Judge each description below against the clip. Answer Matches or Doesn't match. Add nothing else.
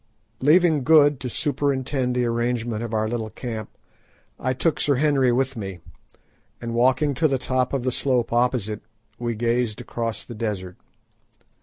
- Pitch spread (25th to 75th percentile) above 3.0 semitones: Doesn't match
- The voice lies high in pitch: Doesn't match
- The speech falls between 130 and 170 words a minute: Matches